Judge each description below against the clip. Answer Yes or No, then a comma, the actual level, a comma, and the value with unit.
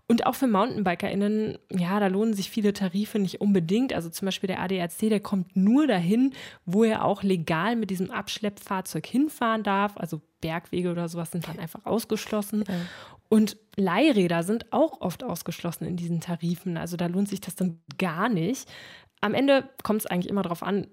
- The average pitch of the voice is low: No, high, 195 Hz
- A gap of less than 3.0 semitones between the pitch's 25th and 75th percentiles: No, average, 3.5 semitones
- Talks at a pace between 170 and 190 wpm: Yes, average, 180 wpm